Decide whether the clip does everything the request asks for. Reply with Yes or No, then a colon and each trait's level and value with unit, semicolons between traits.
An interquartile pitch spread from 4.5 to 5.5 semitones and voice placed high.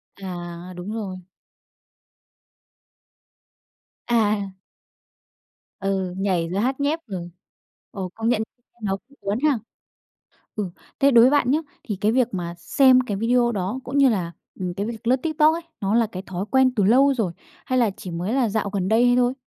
Yes: average, 4.9 semitones; high, 215 Hz